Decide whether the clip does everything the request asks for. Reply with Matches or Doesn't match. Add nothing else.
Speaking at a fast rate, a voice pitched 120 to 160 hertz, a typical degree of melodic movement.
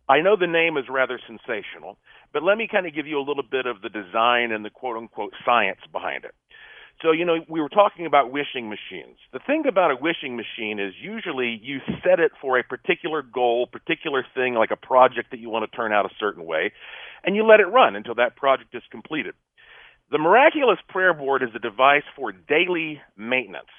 Doesn't match